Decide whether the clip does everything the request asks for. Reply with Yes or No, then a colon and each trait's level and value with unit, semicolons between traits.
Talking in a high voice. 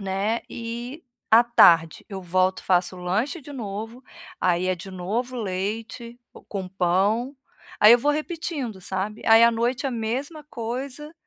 Yes: high, 225 Hz